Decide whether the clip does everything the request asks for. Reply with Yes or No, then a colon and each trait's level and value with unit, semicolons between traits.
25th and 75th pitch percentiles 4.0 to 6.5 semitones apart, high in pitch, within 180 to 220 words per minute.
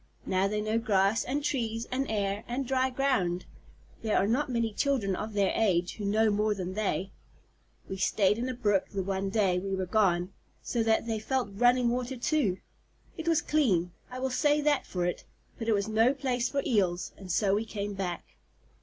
Yes: average, 4.3 semitones; high, 215 Hz; average, 200 wpm